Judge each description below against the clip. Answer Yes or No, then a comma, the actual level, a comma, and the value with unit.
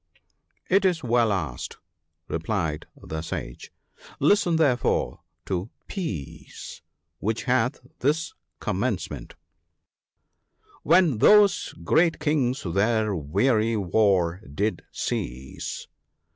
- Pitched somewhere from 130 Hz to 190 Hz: No, low, 110 Hz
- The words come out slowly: Yes, slow, 105 wpm